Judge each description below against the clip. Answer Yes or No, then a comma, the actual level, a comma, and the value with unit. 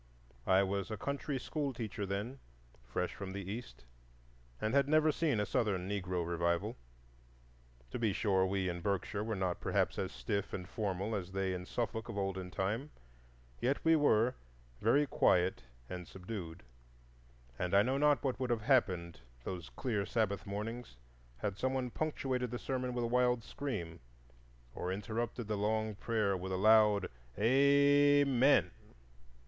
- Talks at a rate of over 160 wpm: No, average, 155 wpm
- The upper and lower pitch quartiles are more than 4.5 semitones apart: Yes, average, 4.9 semitones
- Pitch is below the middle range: Yes, low, 105 Hz